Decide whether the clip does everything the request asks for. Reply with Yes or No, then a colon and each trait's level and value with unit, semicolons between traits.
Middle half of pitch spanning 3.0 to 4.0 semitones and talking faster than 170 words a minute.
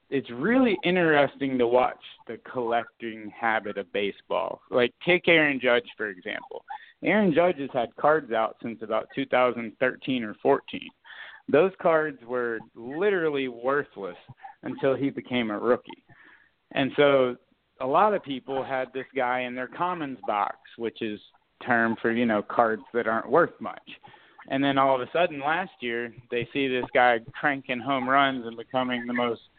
No: average, 3.4 semitones; average, 160 wpm